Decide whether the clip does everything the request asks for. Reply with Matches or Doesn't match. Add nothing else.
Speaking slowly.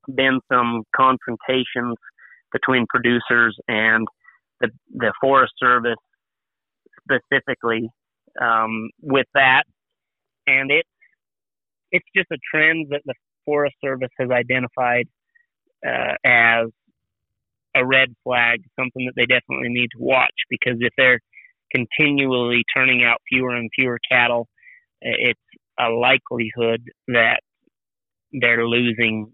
Matches